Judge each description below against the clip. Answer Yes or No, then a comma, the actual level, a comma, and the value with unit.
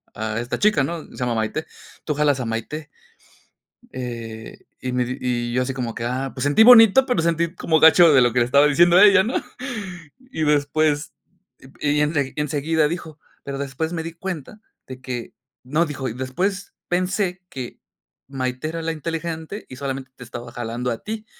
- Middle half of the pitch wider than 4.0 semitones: Yes, average, 4.7 semitones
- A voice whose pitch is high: No, medium, 145 Hz